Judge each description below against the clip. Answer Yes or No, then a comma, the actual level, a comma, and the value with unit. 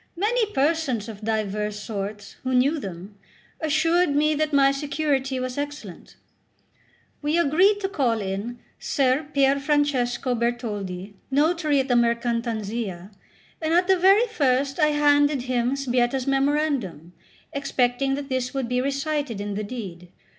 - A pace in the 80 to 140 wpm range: Yes, slow, 135 wpm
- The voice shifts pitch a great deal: No, average, 4.1 semitones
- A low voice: No, very high, 265 Hz